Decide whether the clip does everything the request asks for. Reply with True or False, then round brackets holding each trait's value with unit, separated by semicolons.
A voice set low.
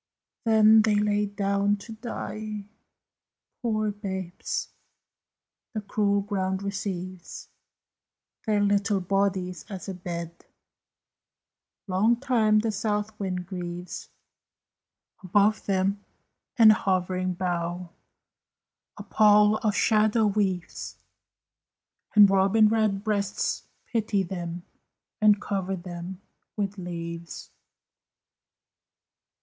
False (200 Hz)